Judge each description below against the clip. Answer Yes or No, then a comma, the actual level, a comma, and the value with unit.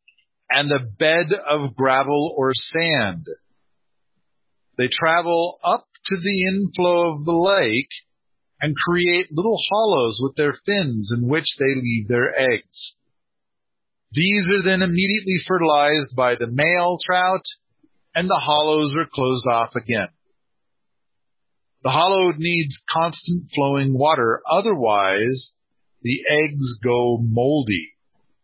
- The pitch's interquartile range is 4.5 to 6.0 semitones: Yes, average, 5.1 semitones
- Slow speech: Yes, slow, 120 wpm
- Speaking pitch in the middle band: Yes, medium, 155 Hz